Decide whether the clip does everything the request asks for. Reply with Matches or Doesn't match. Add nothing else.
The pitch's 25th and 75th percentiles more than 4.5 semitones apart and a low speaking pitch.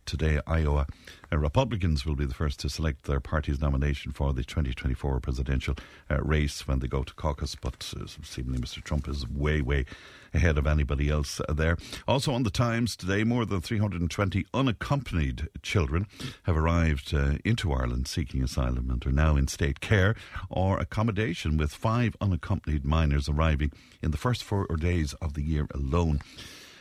Matches